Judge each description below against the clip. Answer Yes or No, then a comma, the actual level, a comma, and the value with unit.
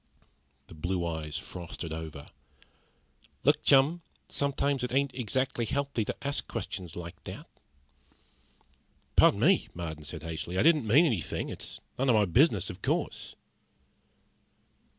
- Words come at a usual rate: No, slow, 130 wpm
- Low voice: Yes, low, 105 Hz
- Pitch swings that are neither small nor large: No, wide, 8.6 semitones